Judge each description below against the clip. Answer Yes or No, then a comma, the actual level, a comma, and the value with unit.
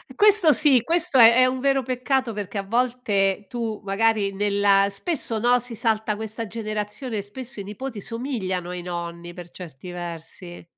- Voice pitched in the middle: No, high, 215 Hz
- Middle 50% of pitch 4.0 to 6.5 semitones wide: Yes, average, 4.3 semitones